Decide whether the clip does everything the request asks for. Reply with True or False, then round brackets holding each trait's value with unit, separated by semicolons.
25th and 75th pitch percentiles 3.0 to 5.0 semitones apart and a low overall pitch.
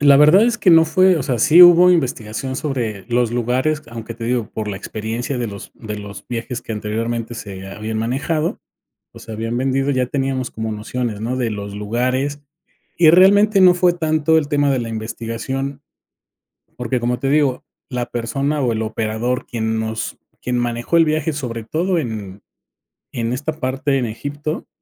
True (4.7 semitones; 125 Hz)